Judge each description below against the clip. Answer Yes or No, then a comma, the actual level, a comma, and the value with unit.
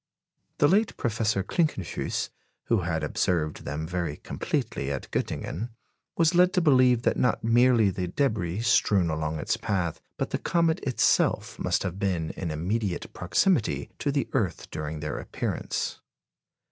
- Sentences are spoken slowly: No, average, 145 wpm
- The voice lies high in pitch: No, low, 100 Hz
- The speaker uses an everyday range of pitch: No, wide, 7.0 semitones